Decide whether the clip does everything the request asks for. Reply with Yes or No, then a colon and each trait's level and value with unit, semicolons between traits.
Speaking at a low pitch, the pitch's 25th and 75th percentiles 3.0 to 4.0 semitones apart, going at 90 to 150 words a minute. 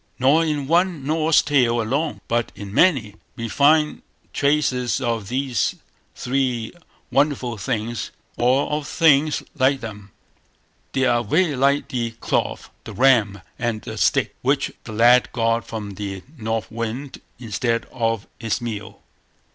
Yes: low, 125 Hz; average, 3.7 semitones; average, 140 wpm